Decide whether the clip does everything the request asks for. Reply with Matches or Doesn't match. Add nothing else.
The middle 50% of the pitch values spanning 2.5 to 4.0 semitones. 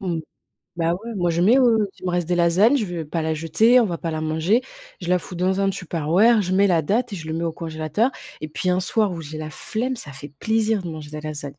Doesn't match